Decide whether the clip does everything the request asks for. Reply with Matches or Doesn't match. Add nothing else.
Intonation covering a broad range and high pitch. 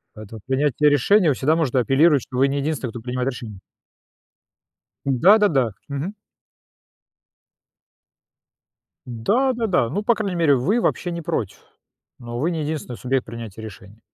Doesn't match